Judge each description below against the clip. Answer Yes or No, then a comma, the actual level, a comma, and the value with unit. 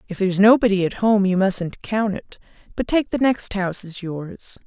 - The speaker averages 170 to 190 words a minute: No, fast, 205 wpm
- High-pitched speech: Yes, high, 200 Hz